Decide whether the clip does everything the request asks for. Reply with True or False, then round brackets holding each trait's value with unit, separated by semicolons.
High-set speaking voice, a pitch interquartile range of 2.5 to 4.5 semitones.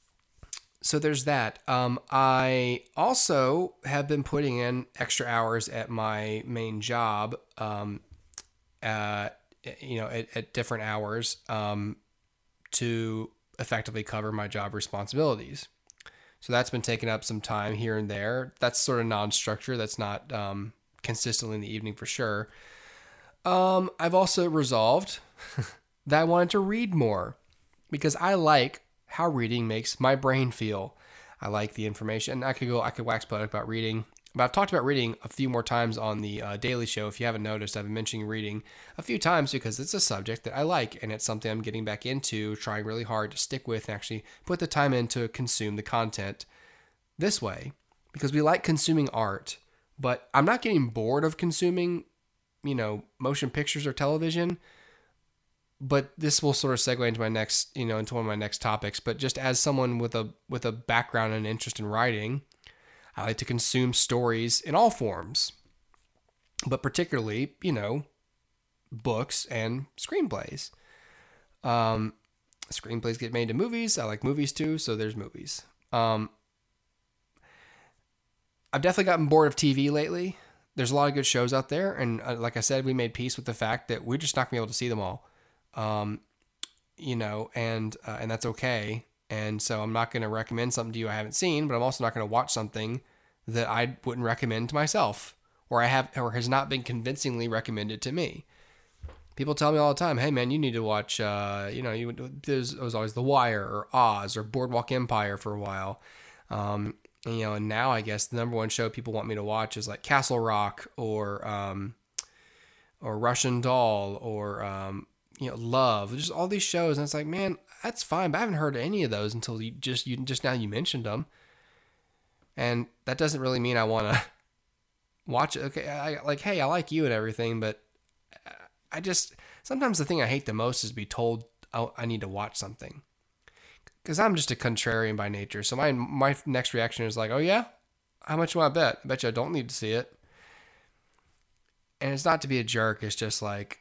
False (120 Hz; 4.0 semitones)